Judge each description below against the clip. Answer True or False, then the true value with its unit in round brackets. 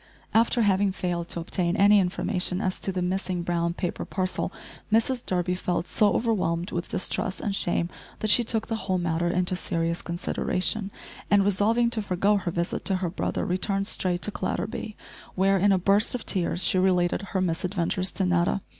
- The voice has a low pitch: False (185 Hz)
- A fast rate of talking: False (180 wpm)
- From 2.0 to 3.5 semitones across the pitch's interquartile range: True (2.5 semitones)